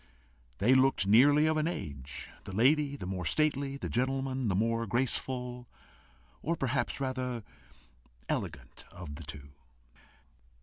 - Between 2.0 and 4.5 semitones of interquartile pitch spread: No, average, 5.3 semitones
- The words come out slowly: Yes, slow, 130 wpm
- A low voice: Yes, low, 125 Hz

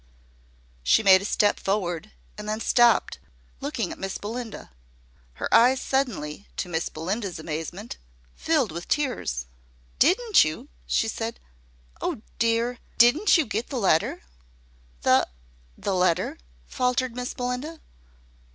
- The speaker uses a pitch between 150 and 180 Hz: No, high, 215 Hz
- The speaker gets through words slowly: Yes, slow, 125 wpm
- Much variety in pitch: Yes, wide, 5.8 semitones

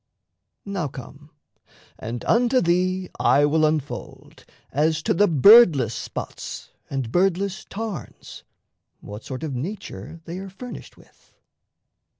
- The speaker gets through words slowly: Yes, slow, 120 wpm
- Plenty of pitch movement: Yes, wide, 5.9 semitones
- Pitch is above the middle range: No, medium, 165 Hz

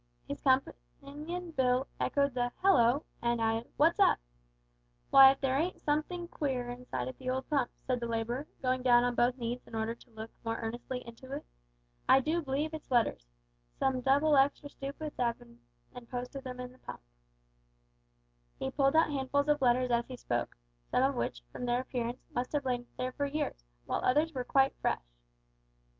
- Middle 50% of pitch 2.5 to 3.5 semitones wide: Yes, average, 2.8 semitones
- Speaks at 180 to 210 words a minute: Yes, average, 185 wpm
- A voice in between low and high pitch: No, very high, 255 Hz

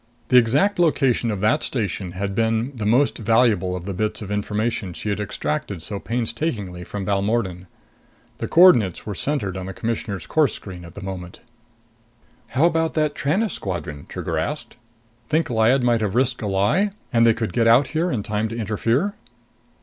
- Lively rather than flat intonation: No, average, 4.7 semitones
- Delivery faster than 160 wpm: Yes, average, 180 wpm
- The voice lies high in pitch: No, low, 110 Hz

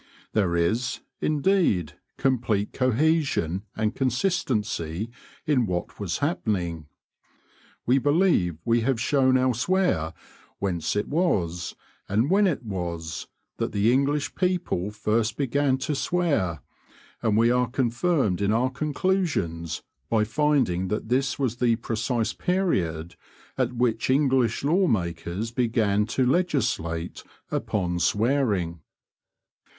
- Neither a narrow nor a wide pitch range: No, wide, 6.7 semitones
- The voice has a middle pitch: No, low, 115 Hz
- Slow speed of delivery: Yes, slow, 115 wpm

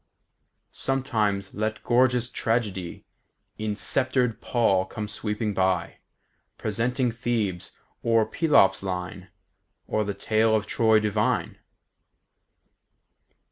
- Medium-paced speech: No, slow, 100 wpm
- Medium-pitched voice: No, low, 110 Hz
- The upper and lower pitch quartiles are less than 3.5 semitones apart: Yes, average, 2.9 semitones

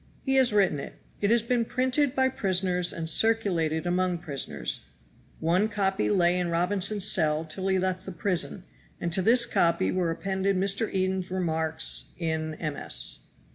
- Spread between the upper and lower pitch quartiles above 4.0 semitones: No, average, 3.4 semitones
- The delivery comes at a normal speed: Yes, average, 160 wpm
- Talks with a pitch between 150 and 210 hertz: Yes, medium, 185 Hz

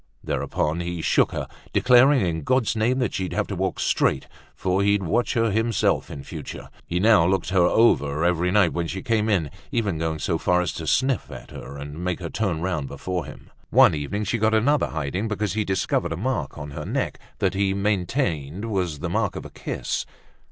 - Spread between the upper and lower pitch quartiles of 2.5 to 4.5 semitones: No, average, 4.9 semitones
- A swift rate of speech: Yes, fast, 210 wpm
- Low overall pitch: Yes, very low, 95 Hz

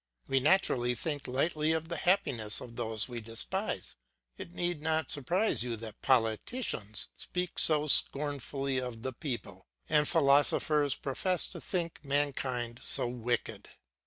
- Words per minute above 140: No, slow, 135 wpm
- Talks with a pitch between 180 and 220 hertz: No, medium, 140 Hz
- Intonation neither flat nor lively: Yes, average, 4.7 semitones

